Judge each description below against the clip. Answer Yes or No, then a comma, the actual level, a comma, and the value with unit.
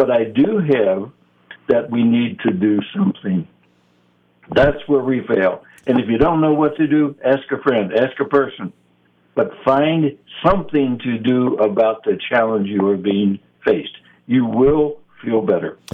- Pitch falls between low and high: No, low, 125 Hz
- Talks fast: No, average, 165 wpm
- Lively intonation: Yes, wide, 5.9 semitones